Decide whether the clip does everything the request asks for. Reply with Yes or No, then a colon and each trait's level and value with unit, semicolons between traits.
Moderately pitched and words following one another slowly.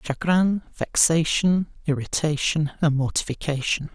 Yes: medium, 155 Hz; slow, 75 wpm